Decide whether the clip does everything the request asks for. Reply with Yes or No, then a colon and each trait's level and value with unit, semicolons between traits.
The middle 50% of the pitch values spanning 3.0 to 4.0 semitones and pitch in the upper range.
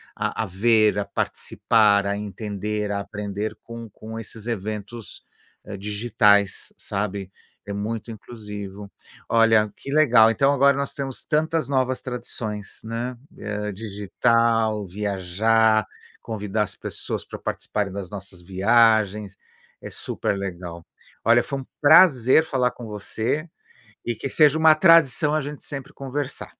No: average, 3.4 semitones; low, 110 Hz